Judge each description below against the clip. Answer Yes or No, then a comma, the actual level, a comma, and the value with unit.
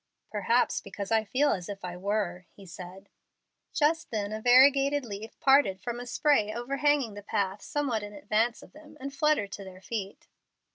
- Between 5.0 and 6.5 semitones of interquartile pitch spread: Yes, wide, 5.6 semitones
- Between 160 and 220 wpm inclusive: Yes, average, 180 wpm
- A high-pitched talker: Yes, high, 220 Hz